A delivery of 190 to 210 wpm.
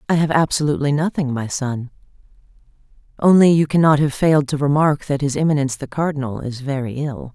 No: average, 170 wpm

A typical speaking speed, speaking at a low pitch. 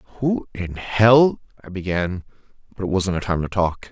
Yes: average, 185 wpm; low, 100 Hz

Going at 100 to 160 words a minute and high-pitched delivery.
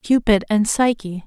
Yes: average, 140 wpm; high, 215 Hz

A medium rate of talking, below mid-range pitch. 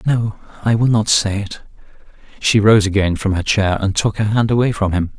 No: fast, 210 wpm; low, 105 Hz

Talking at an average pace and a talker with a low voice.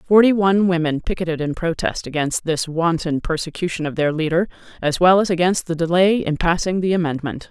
No: average, 185 wpm; medium, 170 Hz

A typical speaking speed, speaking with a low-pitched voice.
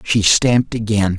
Yes: average, 150 wpm; low, 105 Hz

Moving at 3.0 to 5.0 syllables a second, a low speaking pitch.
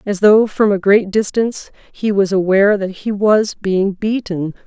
No: 4.5 syllables/s; high, 200 Hz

